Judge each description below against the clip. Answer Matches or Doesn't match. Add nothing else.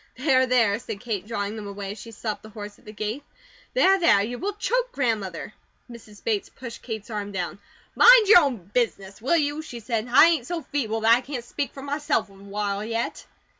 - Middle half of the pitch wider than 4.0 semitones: Matches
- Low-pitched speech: Doesn't match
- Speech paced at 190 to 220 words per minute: Matches